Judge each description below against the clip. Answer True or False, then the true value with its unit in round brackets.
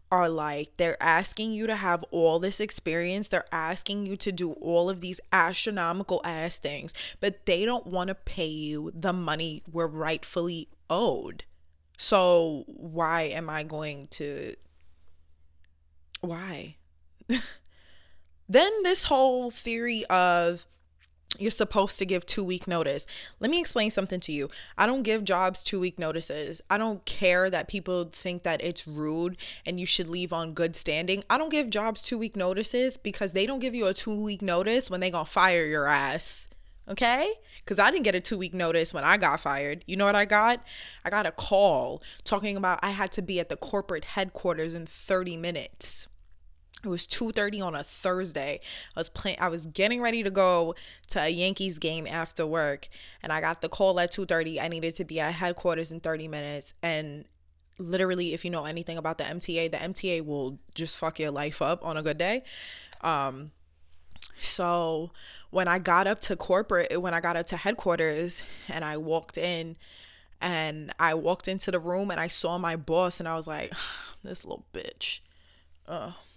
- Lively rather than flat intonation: False (3.6 semitones)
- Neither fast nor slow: True (185 wpm)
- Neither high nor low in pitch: True (170 Hz)